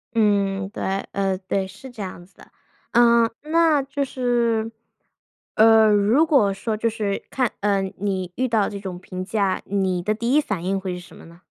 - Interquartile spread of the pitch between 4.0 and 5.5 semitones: No, average, 3.4 semitones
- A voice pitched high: Yes, high, 205 Hz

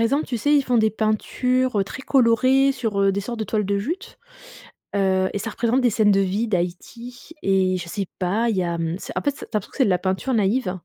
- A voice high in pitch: Yes, high, 215 Hz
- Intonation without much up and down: No, average, 4.5 semitones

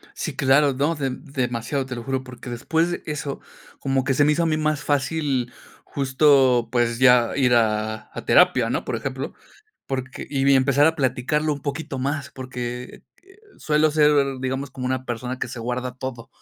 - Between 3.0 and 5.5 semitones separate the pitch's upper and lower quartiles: No, narrow, 2.5 semitones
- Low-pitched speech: Yes, low, 130 Hz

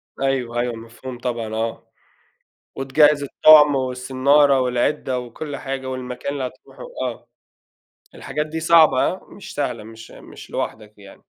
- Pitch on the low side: Yes, low, 130 Hz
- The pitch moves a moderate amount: Yes, average, 3.1 semitones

